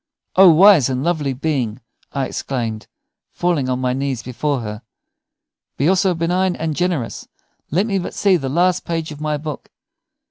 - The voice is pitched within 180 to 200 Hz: No, medium, 150 Hz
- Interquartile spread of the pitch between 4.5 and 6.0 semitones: Yes, average, 5.3 semitones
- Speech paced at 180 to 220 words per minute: No, average, 165 wpm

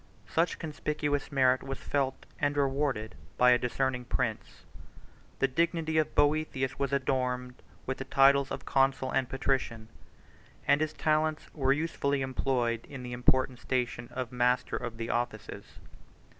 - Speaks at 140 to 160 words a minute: Yes, average, 145 wpm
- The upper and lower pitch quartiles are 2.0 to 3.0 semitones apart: Yes, narrow, 2.4 semitones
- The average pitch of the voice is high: No, low, 135 Hz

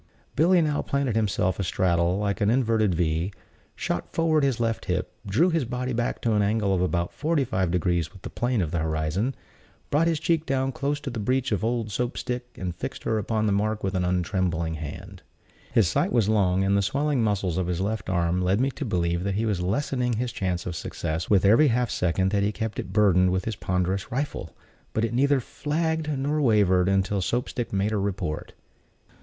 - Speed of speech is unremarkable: No, fast, 210 wpm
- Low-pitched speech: Yes, low, 105 Hz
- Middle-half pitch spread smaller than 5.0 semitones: No, average, 5.3 semitones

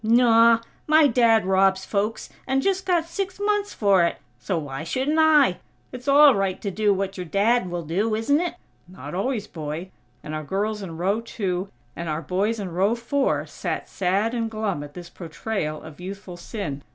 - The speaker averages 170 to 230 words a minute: Yes, average, 190 wpm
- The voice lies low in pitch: No, high, 200 Hz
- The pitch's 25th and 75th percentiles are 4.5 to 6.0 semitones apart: Yes, average, 5.1 semitones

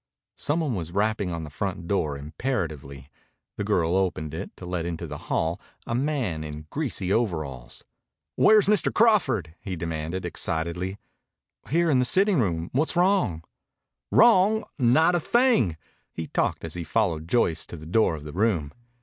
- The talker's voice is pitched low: Yes, very low, 95 Hz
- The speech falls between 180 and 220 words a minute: No, average, 165 wpm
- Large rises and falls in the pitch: Yes, wide, 8.6 semitones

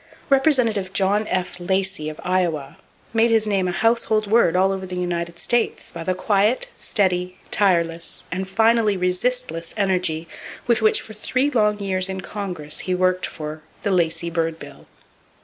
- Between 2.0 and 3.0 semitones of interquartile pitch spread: No, average, 3.4 semitones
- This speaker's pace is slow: No, average, 160 wpm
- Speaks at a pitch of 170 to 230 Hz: Yes, high, 190 Hz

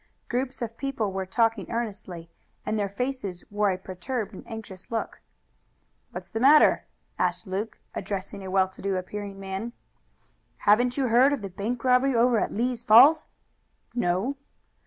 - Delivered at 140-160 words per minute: Yes, average, 155 wpm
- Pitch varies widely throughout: No, average, 4.2 semitones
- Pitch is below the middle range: No, high, 220 Hz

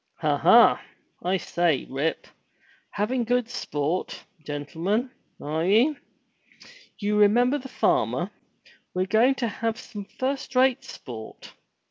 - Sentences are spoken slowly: Yes, slow, 115 wpm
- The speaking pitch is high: Yes, high, 210 Hz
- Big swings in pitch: Yes, wide, 6.7 semitones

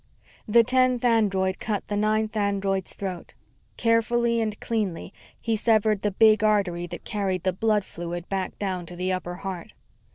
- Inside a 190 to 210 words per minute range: No, average, 160 wpm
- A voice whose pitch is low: No, high, 205 Hz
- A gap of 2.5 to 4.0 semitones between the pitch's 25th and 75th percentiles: Yes, average, 2.8 semitones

